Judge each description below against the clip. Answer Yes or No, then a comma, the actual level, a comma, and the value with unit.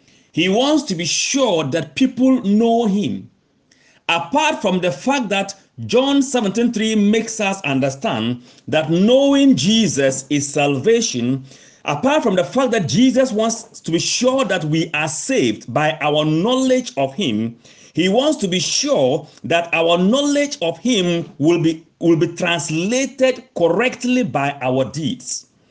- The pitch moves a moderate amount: No, wide, 7.9 semitones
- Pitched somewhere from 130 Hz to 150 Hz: No, high, 190 Hz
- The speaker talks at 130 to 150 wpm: Yes, average, 145 wpm